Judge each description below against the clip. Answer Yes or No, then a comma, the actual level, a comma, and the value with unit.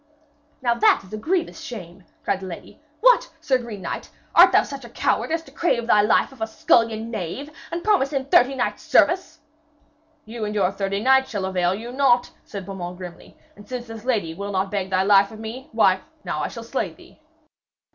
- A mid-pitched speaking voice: No, high, 225 Hz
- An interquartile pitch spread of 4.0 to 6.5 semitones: Yes, average, 5.3 semitones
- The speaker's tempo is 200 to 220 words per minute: Yes, fast, 205 wpm